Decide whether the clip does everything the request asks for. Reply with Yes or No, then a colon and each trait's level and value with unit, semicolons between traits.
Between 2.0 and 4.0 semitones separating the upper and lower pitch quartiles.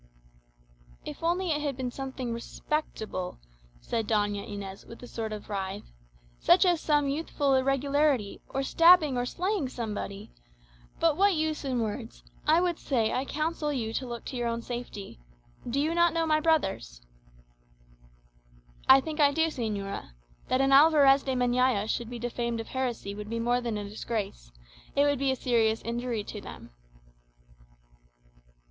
No: average, 4.9 semitones